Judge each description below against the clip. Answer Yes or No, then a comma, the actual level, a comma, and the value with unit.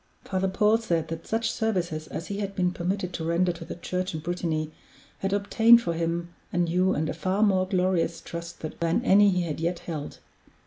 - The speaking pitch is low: No, medium, 180 Hz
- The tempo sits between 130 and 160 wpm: No, fast, 205 wpm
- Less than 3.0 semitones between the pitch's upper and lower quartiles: Yes, narrow, 2.6 semitones